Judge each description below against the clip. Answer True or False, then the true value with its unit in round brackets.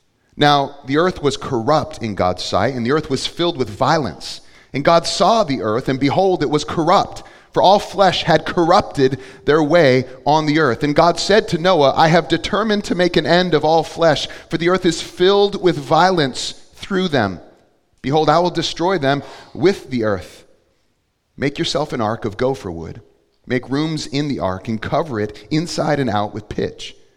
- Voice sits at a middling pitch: True (150 Hz)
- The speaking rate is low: False (190 wpm)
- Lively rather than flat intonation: False (4.8 semitones)